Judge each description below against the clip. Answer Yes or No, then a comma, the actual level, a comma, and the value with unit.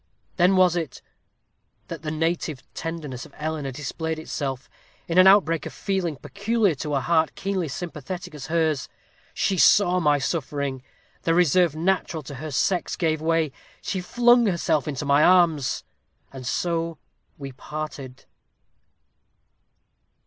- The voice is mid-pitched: Yes, medium, 160 Hz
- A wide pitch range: No, average, 3.6 semitones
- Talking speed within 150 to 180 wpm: No, slow, 135 wpm